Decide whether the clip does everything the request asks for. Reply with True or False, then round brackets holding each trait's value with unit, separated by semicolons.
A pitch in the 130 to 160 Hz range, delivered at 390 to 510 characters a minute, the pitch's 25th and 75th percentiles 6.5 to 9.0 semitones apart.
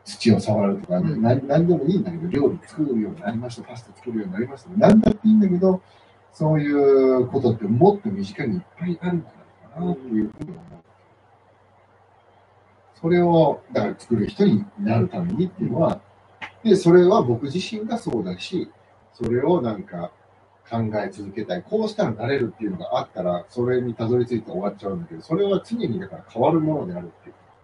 True (135 Hz; 400 characters per minute; 8.4 semitones)